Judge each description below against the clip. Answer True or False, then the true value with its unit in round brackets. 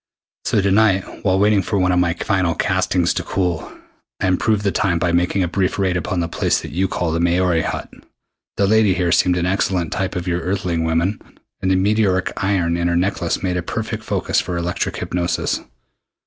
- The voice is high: False (90 Hz)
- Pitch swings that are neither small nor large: False (2.0 semitones)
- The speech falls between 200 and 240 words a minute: True (205 wpm)